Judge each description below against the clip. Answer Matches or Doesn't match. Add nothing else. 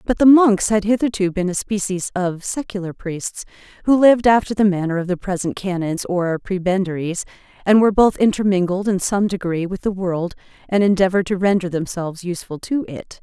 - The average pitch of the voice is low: Doesn't match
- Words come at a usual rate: Matches